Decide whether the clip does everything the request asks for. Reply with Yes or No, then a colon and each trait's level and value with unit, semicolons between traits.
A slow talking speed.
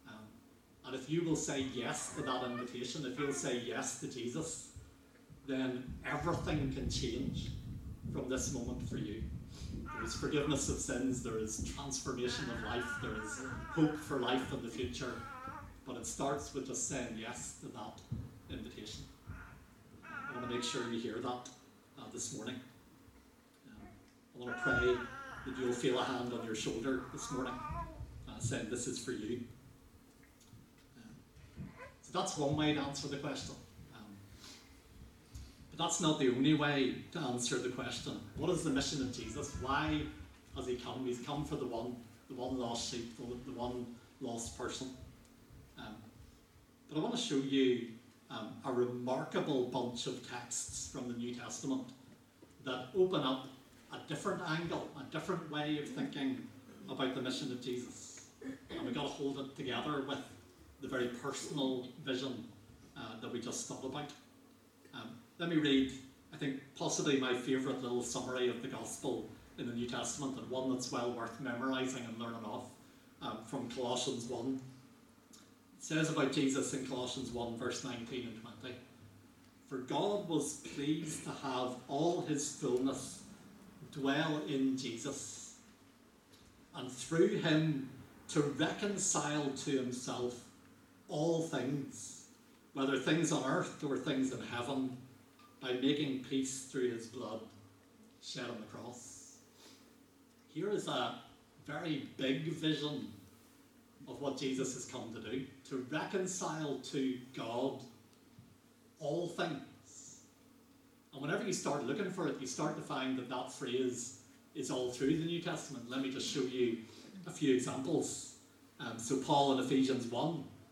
No: average, 155 wpm